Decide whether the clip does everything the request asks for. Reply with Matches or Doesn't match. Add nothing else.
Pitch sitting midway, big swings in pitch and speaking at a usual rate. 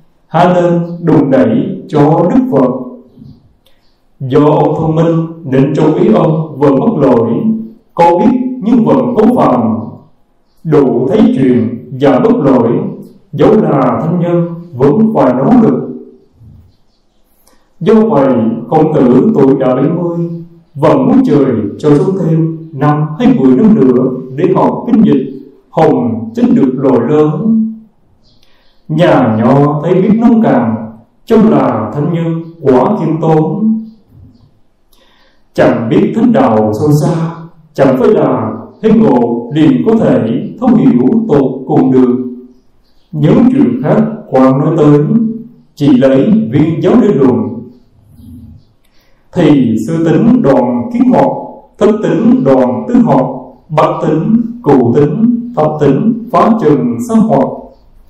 Doesn't match